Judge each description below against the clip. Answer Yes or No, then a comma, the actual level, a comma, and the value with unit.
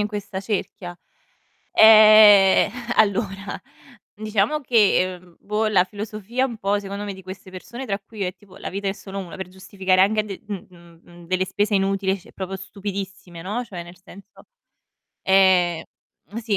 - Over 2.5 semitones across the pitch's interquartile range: No, narrow, 2.0 semitones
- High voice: Yes, high, 195 Hz